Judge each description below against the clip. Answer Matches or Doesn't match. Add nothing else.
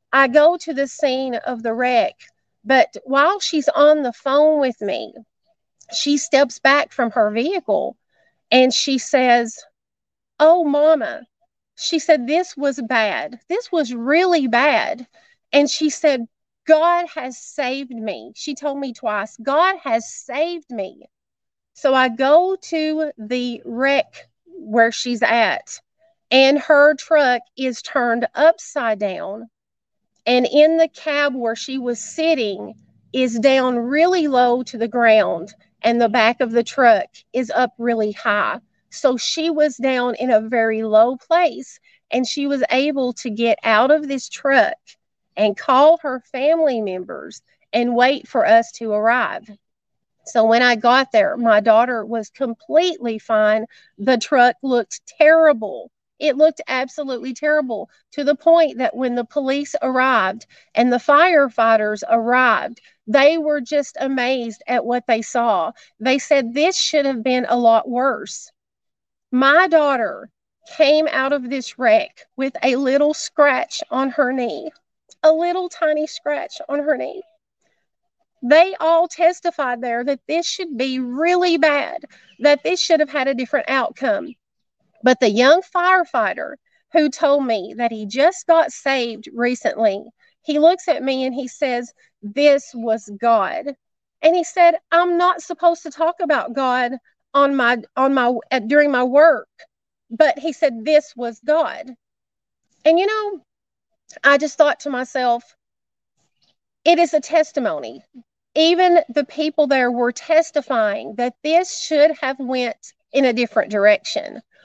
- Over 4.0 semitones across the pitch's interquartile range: Matches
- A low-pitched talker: Doesn't match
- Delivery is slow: Doesn't match